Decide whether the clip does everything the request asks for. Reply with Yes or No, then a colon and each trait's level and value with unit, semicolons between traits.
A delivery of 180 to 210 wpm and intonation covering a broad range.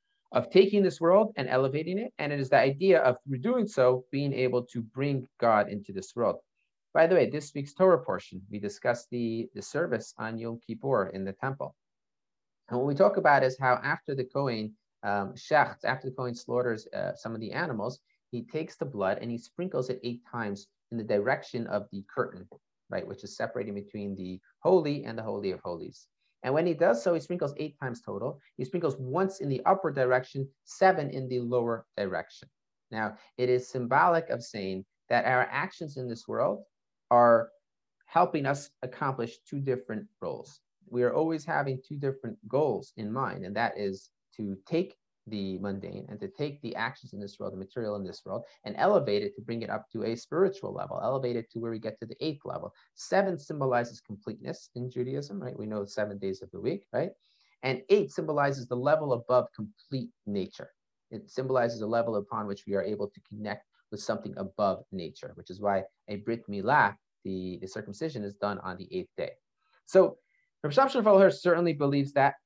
Yes: average, 200 wpm; wide, 5.7 semitones